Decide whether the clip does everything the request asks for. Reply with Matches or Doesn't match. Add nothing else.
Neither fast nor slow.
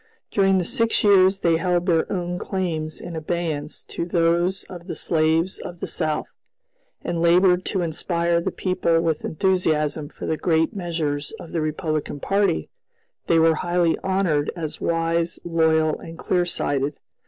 Matches